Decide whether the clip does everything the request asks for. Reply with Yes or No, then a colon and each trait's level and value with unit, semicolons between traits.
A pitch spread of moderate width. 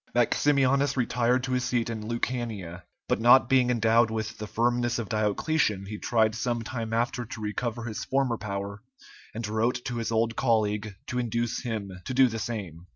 No: narrow, 2.2 semitones